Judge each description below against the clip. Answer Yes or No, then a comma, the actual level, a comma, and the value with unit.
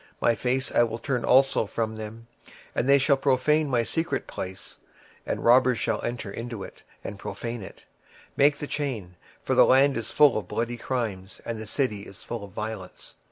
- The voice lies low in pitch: Yes, low, 120 Hz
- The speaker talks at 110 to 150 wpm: No, fast, 205 wpm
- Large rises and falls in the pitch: No, average, 3.6 semitones